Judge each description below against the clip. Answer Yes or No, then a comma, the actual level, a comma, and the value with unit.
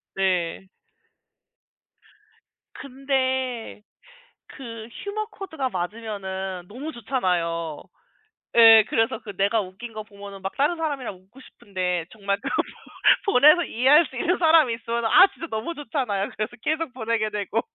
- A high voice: Yes, high, 225 Hz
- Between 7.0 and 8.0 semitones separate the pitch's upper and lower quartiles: No, wide, 5.4 semitones